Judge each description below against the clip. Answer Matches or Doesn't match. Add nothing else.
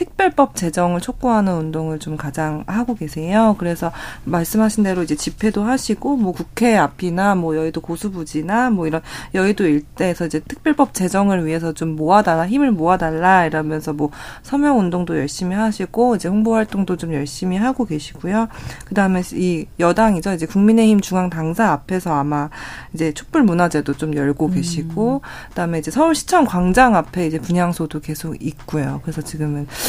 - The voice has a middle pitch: Matches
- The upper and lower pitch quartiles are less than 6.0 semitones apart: Matches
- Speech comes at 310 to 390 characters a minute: Matches